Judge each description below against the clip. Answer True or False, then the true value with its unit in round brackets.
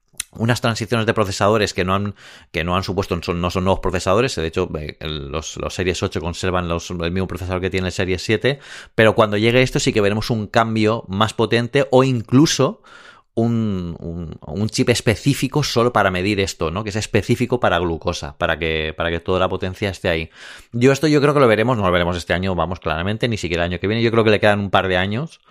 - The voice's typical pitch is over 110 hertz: False (100 Hz)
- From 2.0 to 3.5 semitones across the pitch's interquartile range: False (4.5 semitones)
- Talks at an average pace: False (230 wpm)